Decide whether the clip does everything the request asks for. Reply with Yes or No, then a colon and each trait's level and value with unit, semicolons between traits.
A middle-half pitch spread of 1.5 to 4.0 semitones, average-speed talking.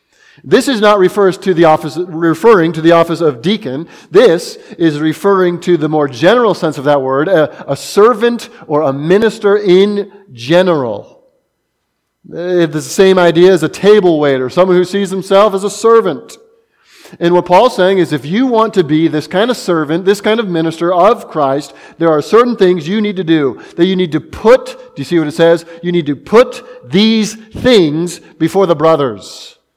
No: average, 4.4 semitones; average, 190 wpm